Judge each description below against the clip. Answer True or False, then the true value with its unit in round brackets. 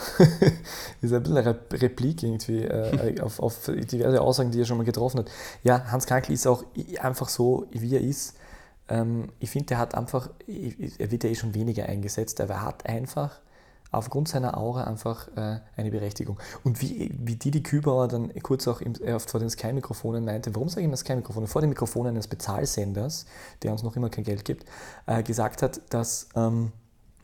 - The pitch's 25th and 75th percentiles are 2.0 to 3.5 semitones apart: True (2.5 semitones)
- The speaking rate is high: True (195 wpm)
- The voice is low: True (120 Hz)